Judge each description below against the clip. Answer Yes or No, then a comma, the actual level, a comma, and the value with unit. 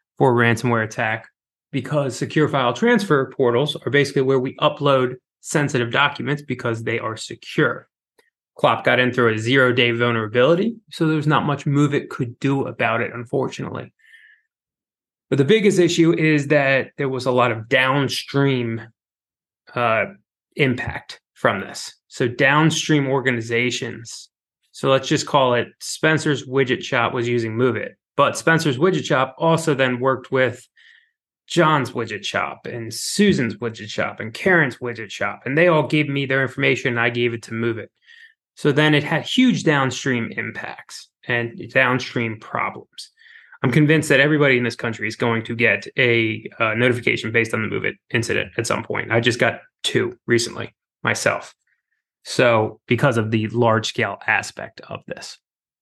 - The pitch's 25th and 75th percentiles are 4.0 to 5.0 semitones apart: Yes, average, 4.3 semitones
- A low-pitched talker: Yes, low, 130 Hz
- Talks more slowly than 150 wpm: No, average, 160 wpm